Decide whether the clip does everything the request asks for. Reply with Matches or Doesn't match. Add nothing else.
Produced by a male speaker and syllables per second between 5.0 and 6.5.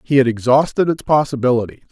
Matches